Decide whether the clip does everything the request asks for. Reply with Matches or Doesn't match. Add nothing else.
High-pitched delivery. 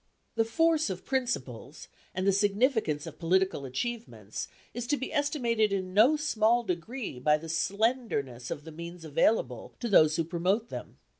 Matches